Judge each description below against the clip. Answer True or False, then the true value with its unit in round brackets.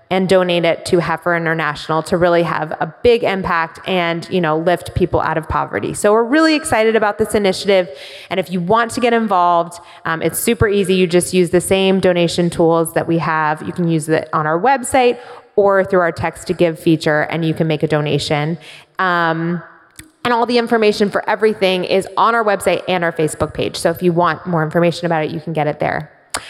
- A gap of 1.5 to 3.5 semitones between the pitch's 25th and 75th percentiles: True (2.8 semitones)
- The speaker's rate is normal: False (215 wpm)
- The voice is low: False (175 Hz)